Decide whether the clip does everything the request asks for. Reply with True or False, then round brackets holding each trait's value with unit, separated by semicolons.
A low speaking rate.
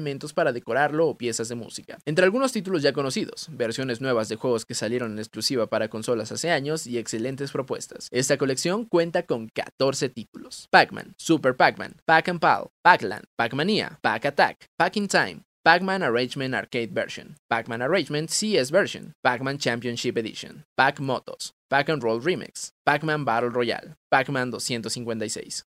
False (145 wpm)